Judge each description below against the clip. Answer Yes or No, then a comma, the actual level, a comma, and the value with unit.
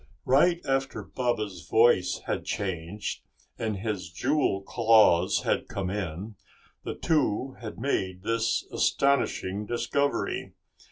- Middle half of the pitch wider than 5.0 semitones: Yes, wide, 5.4 semitones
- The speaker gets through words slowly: Yes, slow, 110 wpm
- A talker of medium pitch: No, low, 110 Hz